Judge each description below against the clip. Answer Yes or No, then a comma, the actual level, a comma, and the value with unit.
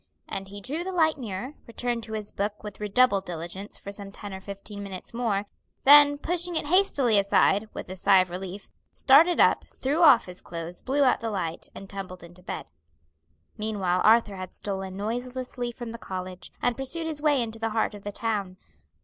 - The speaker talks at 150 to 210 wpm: Yes, average, 195 wpm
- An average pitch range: Yes, average, 4.8 semitones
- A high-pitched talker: Yes, high, 210 Hz